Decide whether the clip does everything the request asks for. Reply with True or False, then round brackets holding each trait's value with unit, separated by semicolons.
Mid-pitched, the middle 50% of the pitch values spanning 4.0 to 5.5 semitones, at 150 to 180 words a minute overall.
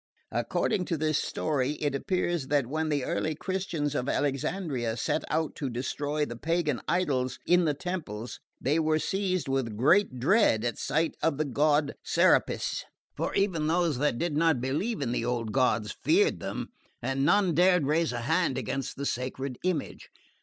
True (150 Hz; 4.5 semitones; 170 wpm)